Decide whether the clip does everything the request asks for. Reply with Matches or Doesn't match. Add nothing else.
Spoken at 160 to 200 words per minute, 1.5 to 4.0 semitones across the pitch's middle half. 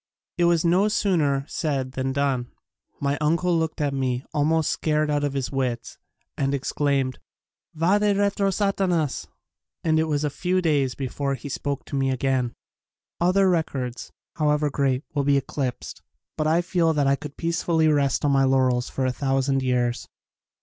Matches